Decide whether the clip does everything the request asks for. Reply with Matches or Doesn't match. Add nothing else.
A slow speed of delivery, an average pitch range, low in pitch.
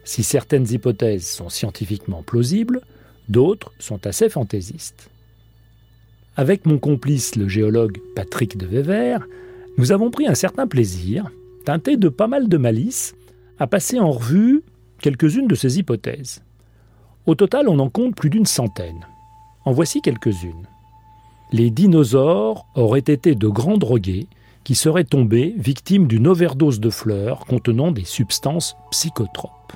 Doesn't match